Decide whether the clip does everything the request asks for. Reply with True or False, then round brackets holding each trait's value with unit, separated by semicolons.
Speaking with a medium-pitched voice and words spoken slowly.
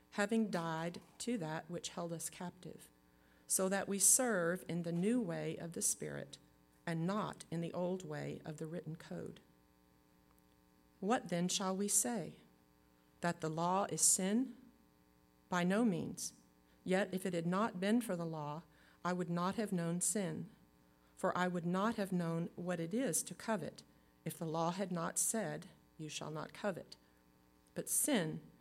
False (170 Hz; 170 wpm)